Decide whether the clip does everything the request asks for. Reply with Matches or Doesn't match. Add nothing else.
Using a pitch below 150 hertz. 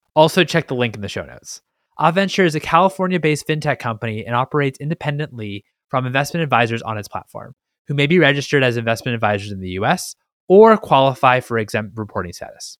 Matches